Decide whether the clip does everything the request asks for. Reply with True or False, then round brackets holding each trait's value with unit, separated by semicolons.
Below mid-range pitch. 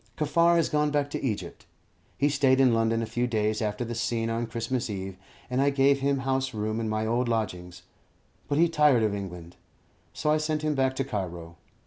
True (120 Hz)